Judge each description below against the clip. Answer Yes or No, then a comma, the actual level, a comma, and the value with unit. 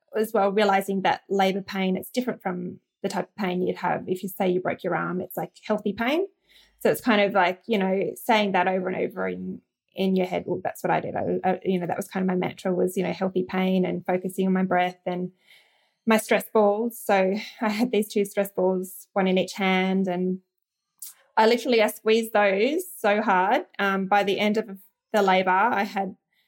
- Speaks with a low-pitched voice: No, high, 195 Hz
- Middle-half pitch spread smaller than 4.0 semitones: Yes, narrow, 2.4 semitones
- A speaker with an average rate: No, fast, 225 wpm